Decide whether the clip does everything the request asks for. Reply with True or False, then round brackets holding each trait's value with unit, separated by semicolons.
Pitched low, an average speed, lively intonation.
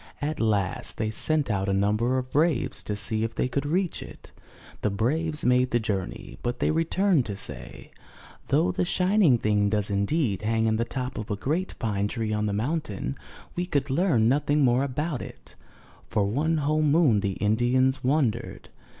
True (120 Hz; 185 wpm; 6.1 semitones)